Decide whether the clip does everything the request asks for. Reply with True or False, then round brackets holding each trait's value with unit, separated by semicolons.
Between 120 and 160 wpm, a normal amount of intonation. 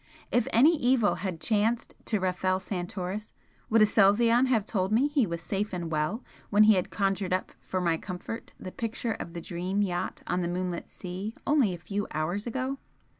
False (185 wpm; 4.0 semitones)